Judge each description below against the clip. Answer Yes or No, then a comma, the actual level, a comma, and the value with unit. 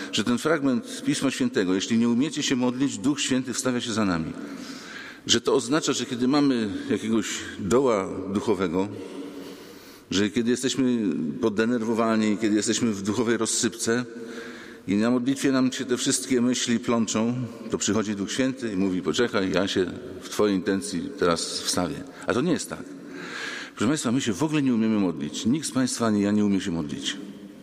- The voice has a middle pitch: No, low, 115 Hz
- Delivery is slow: No, average, 175 wpm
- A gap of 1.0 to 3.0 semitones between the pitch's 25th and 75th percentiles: No, average, 3.4 semitones